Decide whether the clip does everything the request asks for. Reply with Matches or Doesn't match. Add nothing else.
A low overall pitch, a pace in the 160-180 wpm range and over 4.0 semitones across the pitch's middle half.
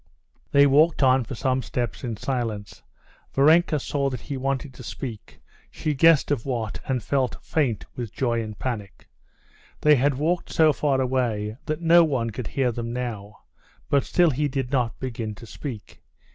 Doesn't match